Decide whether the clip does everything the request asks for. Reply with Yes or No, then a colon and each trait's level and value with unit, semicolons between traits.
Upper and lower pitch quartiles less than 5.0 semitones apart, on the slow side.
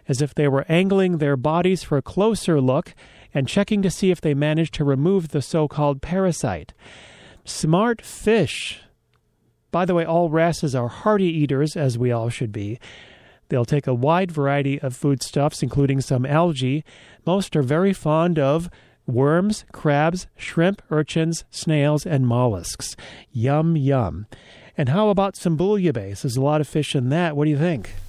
No: average, 4.1 semitones; average, 170 wpm